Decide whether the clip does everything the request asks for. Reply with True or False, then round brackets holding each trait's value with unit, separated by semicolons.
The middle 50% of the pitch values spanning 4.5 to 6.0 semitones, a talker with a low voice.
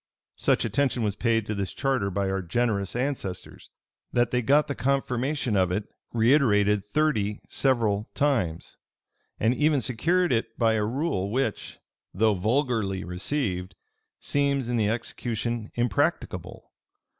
True (4.9 semitones; 115 Hz)